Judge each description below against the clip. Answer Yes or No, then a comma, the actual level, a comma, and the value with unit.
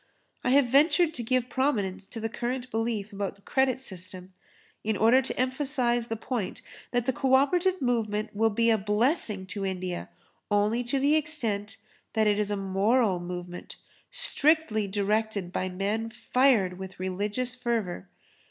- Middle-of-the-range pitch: No, high, 225 Hz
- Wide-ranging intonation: No, average, 4.4 semitones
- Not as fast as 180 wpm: Yes, average, 155 wpm